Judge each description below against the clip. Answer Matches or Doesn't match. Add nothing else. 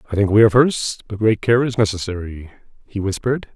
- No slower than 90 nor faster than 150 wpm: Doesn't match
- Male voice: Matches